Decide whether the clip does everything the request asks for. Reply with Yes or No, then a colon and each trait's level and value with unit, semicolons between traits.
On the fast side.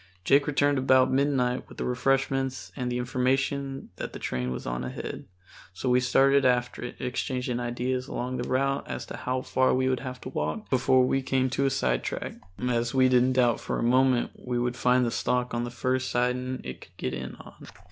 Yes: fast, 210 wpm